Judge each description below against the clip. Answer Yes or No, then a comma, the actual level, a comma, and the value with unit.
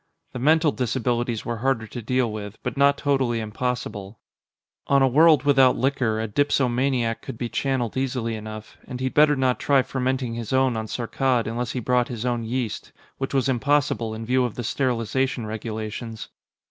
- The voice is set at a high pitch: No, low, 125 Hz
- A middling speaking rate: Yes, average, 175 wpm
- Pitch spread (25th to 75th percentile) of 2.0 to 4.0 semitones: Yes, average, 2.8 semitones